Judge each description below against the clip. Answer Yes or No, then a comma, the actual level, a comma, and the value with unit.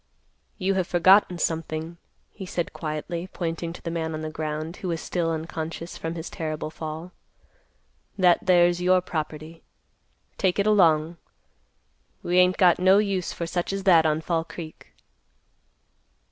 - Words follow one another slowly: No, average, 150 wpm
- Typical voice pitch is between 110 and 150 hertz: No, medium, 170 Hz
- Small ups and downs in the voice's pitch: Yes, narrow, 2.2 semitones